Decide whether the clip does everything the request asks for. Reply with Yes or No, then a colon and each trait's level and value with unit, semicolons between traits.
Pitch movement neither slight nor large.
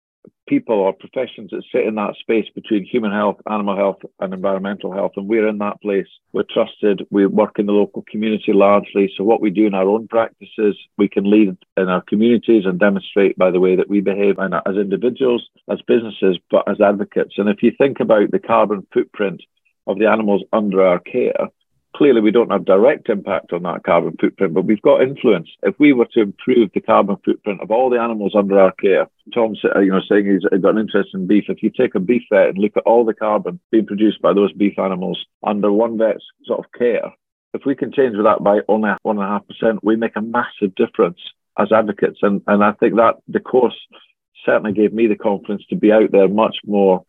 No: narrow, 2.0 semitones